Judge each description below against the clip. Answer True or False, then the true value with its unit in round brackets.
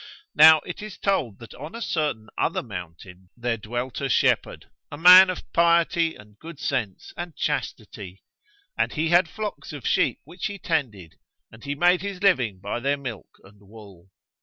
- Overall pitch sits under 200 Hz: True (140 Hz)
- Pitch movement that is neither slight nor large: False (8.1 semitones)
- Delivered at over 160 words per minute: True (175 wpm)